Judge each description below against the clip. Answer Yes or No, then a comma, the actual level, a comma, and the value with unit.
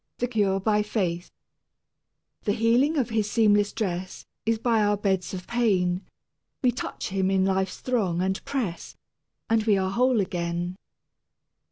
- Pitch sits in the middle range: No, high, 205 Hz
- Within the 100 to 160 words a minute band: Yes, average, 155 wpm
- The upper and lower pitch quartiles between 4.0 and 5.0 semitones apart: No, average, 3.3 semitones